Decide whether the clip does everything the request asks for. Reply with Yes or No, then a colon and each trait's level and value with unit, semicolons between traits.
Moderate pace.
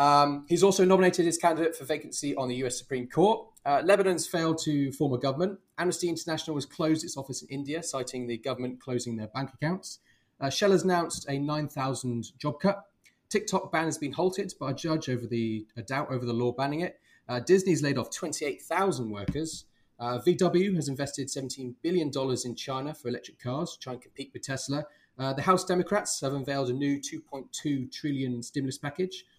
Yes: average, 190 wpm